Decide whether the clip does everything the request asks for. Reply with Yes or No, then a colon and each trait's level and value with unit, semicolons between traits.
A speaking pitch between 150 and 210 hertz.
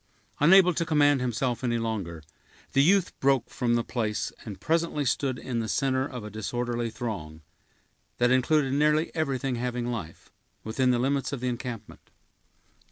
No: low, 125 Hz